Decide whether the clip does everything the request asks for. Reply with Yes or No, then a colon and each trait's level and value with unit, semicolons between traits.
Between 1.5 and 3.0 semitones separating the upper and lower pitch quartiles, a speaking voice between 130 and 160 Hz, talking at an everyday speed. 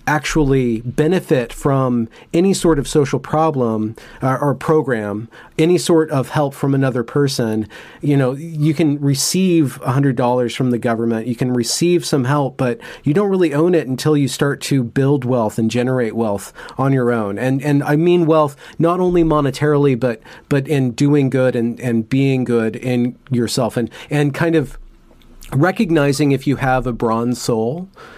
No: average, 3.7 semitones; low, 135 Hz; average, 170 wpm